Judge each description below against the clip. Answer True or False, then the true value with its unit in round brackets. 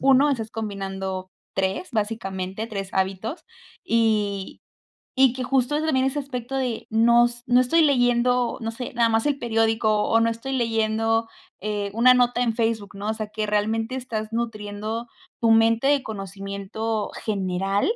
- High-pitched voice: True (225 Hz)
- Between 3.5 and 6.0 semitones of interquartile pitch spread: False (2.9 semitones)